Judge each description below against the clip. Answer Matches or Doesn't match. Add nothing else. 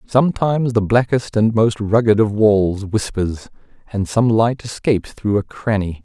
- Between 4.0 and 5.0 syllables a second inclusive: Matches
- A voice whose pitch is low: Matches